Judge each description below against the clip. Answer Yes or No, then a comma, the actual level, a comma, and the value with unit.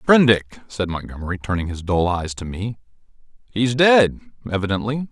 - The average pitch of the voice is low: Yes, low, 105 Hz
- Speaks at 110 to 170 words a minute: Yes, average, 140 wpm